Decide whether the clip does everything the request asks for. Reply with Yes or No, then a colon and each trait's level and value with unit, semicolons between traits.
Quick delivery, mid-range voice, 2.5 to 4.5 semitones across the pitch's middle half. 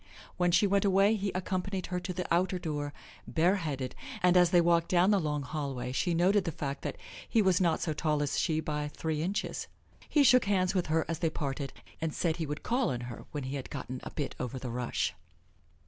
Yes: fast, 225 wpm; medium, 165 Hz; average, 4.0 semitones